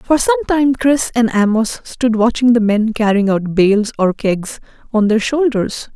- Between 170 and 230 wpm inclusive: Yes, average, 180 wpm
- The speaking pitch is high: Yes, high, 230 Hz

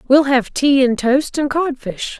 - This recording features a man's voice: No, female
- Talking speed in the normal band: Yes, average, 190 wpm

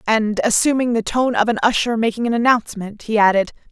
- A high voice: Yes, high, 225 Hz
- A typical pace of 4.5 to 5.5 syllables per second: No, 6.0 syllables/s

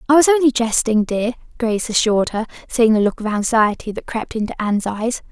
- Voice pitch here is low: No, high, 230 Hz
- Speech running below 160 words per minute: No, fast, 205 wpm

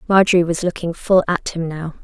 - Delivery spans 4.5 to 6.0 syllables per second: Yes, 5.7 syllables/s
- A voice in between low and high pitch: Yes, medium, 175 Hz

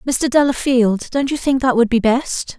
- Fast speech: Yes, fast, 210 wpm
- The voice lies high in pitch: Yes, very high, 250 Hz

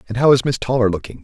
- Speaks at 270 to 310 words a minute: Yes, fast, 290 wpm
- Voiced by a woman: No, male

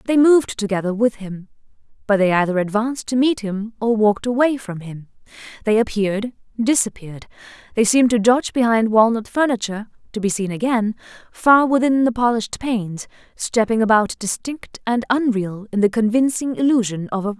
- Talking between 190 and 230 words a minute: No, average, 165 wpm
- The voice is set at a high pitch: Yes, high, 225 Hz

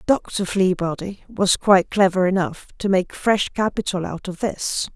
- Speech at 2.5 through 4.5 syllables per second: Yes, 4.4 syllables/s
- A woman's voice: Yes, female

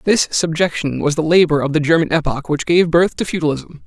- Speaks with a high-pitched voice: No, medium, 160 Hz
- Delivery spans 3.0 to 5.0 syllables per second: No, 5.5 syllables/s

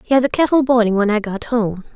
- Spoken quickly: Yes, fast, 275 wpm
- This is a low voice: No, high, 230 Hz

